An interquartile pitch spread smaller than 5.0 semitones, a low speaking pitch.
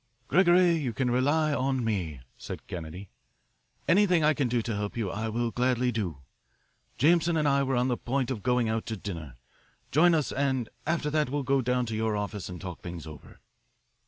No: wide, 5.5 semitones; low, 125 Hz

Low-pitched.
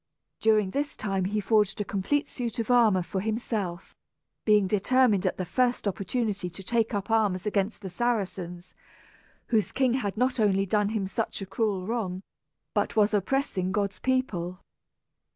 No: high, 210 Hz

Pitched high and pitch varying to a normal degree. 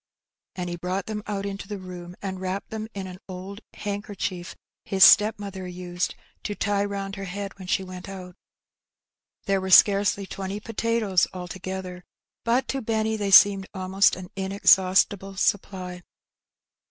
No: high, 195 Hz; narrow, 1.7 semitones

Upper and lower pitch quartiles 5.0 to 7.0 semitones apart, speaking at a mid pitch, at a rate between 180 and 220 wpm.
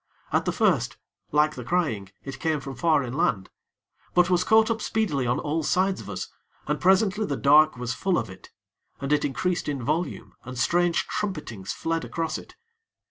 Yes: wide, 5.5 semitones; medium, 155 Hz; average, 185 wpm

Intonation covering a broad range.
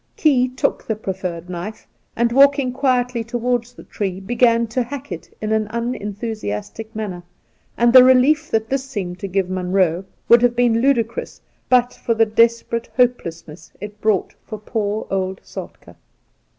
No: average, 3.9 semitones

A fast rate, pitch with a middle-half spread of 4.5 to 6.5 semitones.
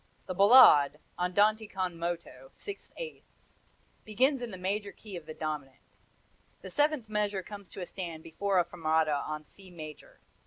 No: average, 160 wpm; average, 4.8 semitones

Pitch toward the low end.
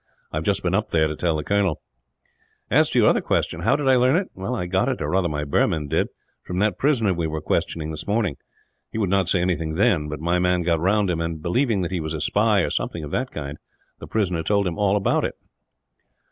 Yes: very low, 90 Hz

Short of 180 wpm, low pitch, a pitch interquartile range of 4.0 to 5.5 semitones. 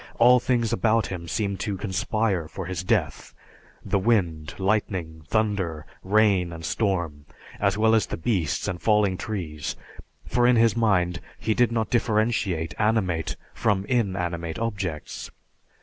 Yes: average, 140 wpm; low, 100 Hz; average, 4.4 semitones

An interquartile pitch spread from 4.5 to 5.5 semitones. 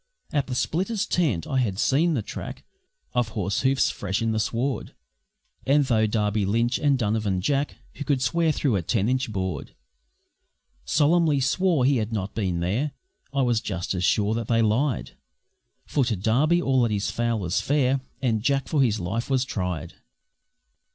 Yes: average, 4.9 semitones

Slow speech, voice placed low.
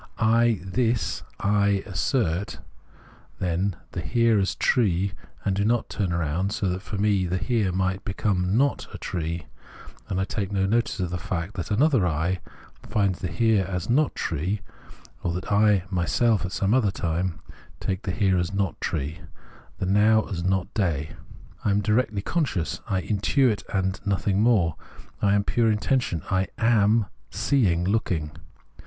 No: average, 165 wpm; low, 100 Hz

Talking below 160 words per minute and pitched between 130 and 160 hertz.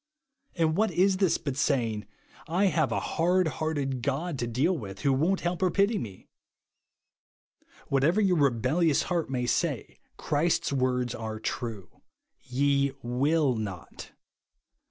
Yes: average, 150 wpm; medium, 140 Hz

